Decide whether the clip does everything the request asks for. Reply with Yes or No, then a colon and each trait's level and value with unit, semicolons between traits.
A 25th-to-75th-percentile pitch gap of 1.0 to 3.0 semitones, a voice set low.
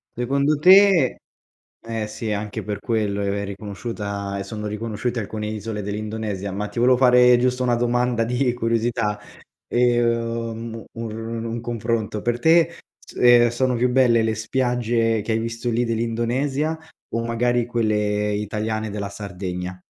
Yes: narrow, 2.5 semitones; low, 115 Hz